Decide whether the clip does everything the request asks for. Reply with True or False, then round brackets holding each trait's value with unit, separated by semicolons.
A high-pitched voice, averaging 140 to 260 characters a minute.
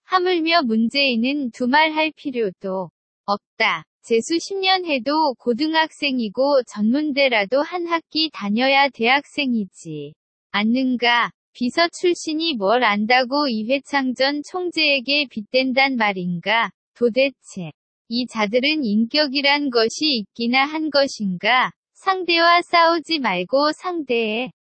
True (270 Hz; 240 characters per minute)